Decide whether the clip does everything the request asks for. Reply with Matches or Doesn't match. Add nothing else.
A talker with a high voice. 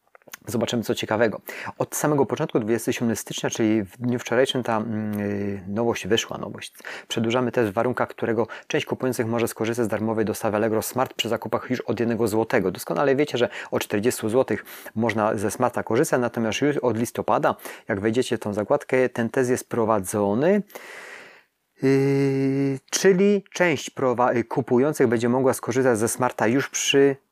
Doesn't match